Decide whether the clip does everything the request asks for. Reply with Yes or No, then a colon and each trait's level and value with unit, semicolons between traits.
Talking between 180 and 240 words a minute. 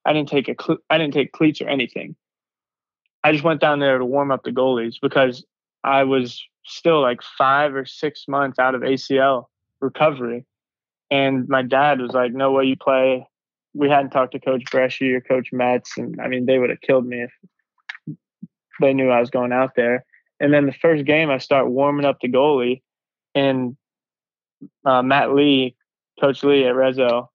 Yes: average, 190 wpm